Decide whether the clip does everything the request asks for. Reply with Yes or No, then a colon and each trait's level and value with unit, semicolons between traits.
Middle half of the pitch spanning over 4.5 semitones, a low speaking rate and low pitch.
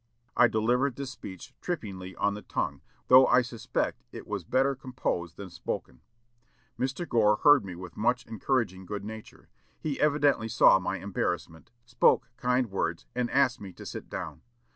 No: average, 5.2 semitones; average, 165 wpm; low, 115 Hz